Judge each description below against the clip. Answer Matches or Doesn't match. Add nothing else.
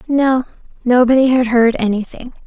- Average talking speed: Doesn't match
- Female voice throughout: Matches